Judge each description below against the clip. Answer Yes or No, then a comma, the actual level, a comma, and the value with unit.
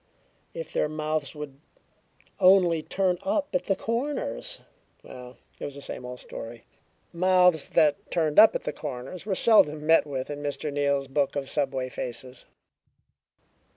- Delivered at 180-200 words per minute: No, average, 155 wpm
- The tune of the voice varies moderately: Yes, average, 5.0 semitones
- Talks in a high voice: No, medium, 150 Hz